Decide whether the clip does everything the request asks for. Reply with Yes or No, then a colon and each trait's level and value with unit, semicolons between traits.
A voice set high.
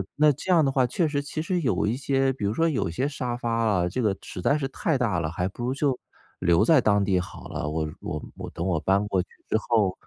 No: low, 120 Hz